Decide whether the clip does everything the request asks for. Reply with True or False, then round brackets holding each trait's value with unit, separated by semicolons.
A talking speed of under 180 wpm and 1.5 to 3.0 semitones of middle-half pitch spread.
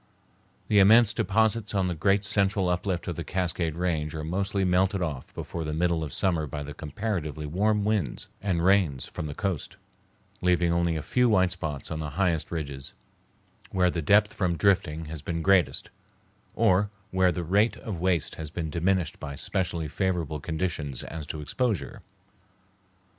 False (170 wpm; 3.7 semitones)